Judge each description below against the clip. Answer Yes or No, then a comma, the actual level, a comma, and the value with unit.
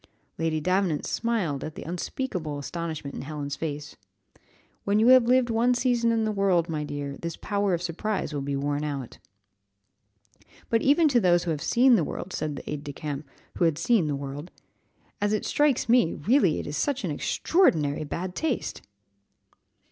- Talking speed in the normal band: Yes, average, 180 wpm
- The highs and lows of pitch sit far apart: Yes, wide, 7.5 semitones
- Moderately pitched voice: Yes, medium, 170 Hz